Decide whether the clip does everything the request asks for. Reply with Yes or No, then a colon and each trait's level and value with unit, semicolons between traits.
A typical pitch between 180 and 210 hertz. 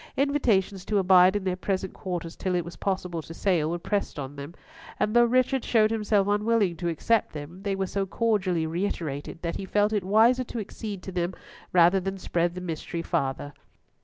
Yes: high, 190 Hz